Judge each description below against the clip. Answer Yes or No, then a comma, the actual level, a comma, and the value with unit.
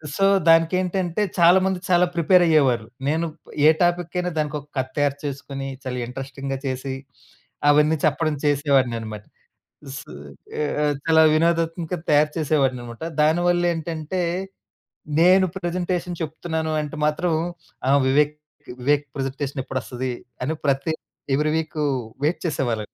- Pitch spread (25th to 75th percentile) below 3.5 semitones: No, average, 3.8 semitones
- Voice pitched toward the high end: No, medium, 150 Hz